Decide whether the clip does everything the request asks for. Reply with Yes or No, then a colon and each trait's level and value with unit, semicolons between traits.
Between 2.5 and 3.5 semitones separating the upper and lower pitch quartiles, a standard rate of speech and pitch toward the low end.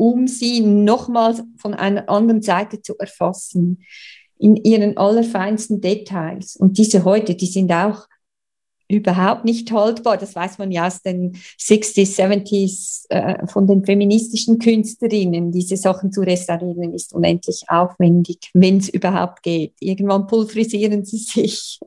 No: average, 2.8 semitones; average, 135 wpm; high, 200 Hz